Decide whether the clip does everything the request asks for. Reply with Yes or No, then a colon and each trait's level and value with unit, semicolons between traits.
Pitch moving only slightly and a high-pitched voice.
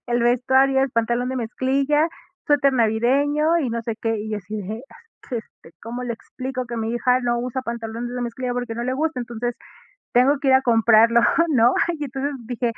Yes: narrow, 2.3 semitones; high, 245 Hz